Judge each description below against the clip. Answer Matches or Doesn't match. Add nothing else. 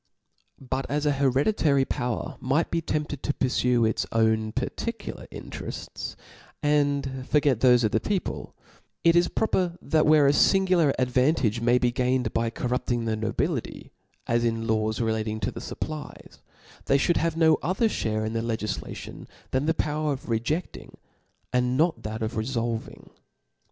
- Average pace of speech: Matches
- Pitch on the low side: Matches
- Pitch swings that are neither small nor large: Matches